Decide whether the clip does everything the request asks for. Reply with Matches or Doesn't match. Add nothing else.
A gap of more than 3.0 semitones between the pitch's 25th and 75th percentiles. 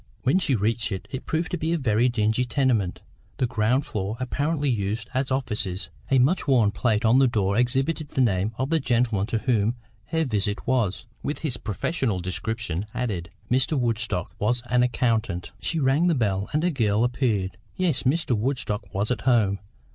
Matches